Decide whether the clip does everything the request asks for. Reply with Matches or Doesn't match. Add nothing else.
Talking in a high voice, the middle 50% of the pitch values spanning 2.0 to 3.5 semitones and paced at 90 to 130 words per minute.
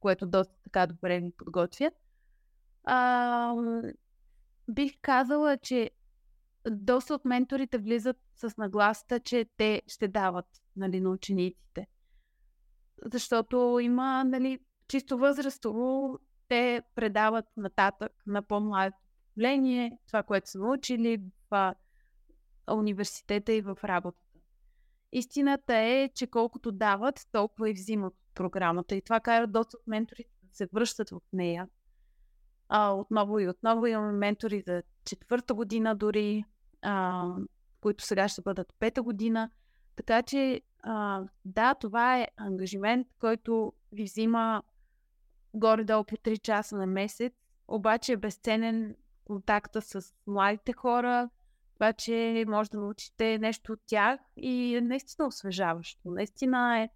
Matches